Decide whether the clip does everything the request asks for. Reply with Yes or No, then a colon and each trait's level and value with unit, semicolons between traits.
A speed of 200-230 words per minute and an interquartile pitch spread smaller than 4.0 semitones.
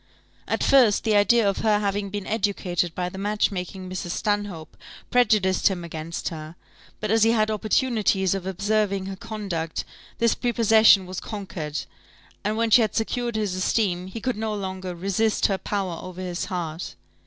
No: average, 170 wpm; average, 2.9 semitones